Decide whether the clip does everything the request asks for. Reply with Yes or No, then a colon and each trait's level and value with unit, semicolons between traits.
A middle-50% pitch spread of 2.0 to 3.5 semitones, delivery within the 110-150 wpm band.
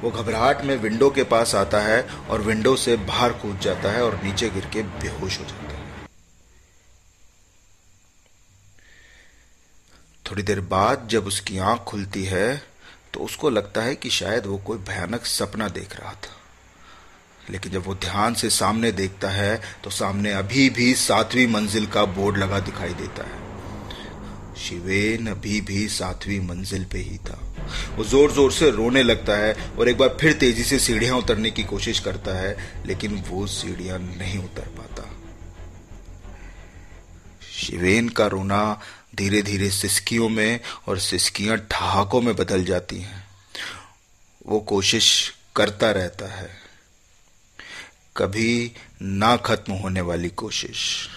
Yes: average, 2.9 semitones; average, 145 wpm